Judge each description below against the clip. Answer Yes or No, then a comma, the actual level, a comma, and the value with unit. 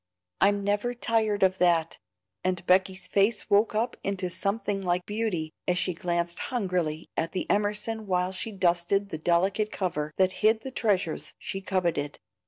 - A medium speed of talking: Yes, average, 160 wpm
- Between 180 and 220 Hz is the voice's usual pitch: Yes, high, 190 Hz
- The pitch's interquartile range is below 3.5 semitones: Yes, average, 2.9 semitones